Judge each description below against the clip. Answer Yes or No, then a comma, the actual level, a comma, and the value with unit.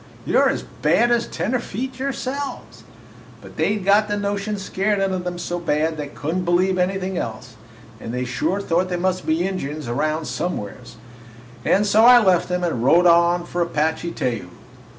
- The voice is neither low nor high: Yes, medium, 180 Hz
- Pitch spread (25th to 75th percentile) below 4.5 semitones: Yes, average, 4.1 semitones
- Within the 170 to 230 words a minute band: Yes, average, 180 wpm